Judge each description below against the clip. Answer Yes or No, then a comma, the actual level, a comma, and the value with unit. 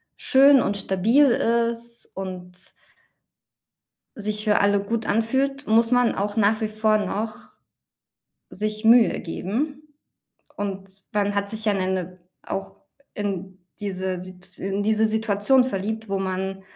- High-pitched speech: Yes, high, 210 Hz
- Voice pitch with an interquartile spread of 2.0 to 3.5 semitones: Yes, average, 2.9 semitones